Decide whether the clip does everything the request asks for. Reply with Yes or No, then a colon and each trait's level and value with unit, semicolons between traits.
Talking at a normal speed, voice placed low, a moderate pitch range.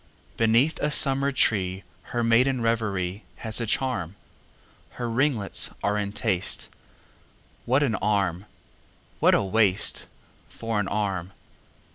No: slow, 95 wpm; low, 110 Hz; average, 3.5 semitones